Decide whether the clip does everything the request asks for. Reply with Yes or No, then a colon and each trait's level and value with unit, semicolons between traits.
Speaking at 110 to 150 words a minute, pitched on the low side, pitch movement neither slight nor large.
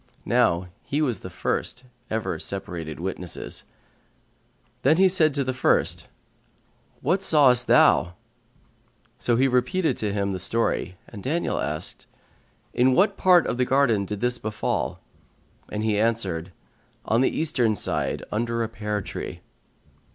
Yes: average, 140 wpm; low, 115 Hz; average, 4.4 semitones